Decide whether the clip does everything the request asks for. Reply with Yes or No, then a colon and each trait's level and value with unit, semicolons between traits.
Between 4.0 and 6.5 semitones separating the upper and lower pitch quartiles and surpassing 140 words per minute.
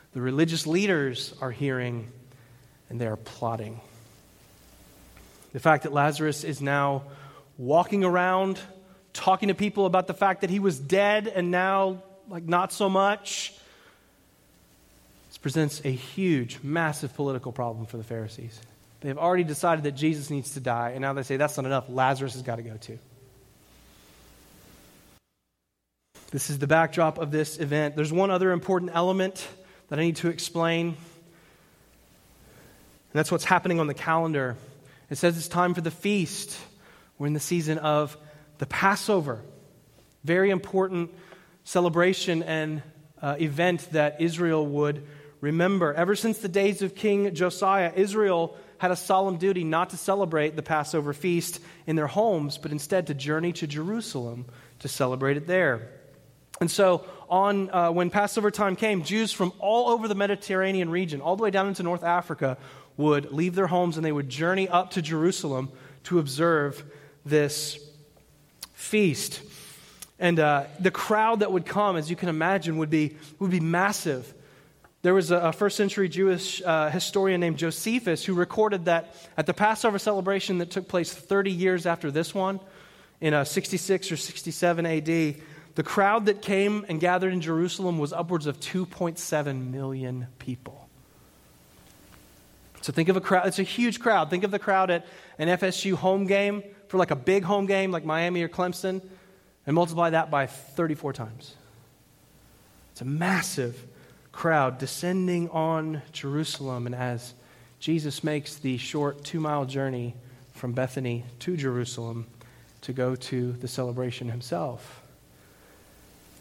Yes: average, 5.1 semitones; average, 155 wpm